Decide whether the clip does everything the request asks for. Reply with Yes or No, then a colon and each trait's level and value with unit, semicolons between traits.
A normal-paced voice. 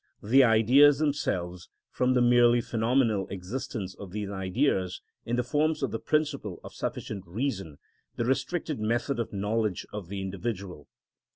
Yes: average, 155 wpm